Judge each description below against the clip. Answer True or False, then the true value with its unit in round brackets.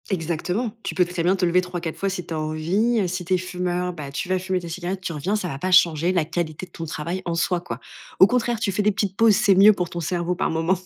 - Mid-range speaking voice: True (180 Hz)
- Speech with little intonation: True (2.1 semitones)